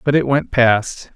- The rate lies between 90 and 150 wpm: No, fast, 205 wpm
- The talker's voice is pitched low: Yes, low, 125 Hz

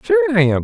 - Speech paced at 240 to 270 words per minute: No, fast, 285 wpm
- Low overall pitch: No, medium, 160 Hz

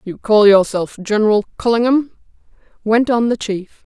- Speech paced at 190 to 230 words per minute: No, slow, 135 wpm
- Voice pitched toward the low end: No, high, 220 Hz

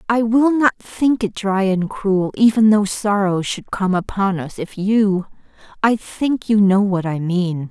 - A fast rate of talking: No, average, 185 wpm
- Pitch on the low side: No, high, 200 Hz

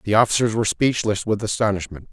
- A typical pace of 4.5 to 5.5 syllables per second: No, 6.5 syllables/s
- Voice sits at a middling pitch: No, low, 105 Hz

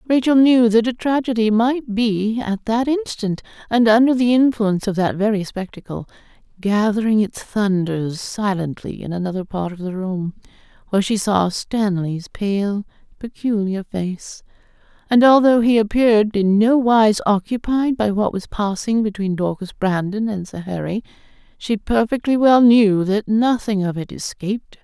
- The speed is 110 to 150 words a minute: Yes, average, 145 wpm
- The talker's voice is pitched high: Yes, high, 215 Hz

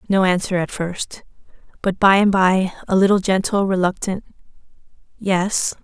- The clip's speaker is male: No, female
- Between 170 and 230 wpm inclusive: No, slow, 135 wpm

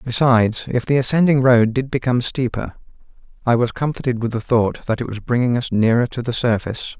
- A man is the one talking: Yes, male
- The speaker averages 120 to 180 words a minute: No, average, 195 wpm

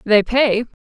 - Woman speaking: Yes, female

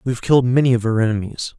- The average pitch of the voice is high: No, low, 120 Hz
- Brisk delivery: Yes, fast, 265 wpm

